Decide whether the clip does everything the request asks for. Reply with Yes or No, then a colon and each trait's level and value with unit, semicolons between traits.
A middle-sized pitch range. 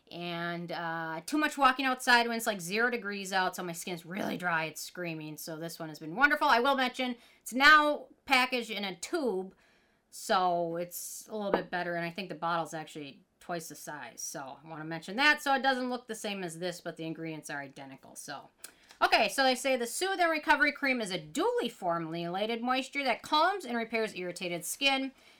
No: wide, 7.4 semitones